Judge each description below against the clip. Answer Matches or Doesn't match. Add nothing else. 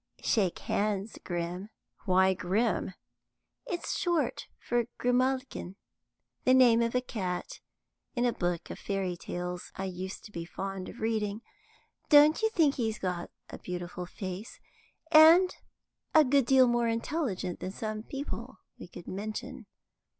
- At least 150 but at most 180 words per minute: Doesn't match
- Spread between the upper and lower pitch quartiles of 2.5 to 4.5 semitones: Doesn't match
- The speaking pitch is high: Matches